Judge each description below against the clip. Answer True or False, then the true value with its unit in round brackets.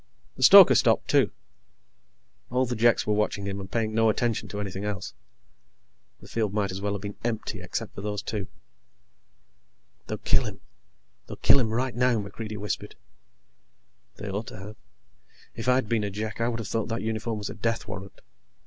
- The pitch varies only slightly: True (2.1 semitones)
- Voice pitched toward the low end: True (110 Hz)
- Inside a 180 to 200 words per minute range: True (185 wpm)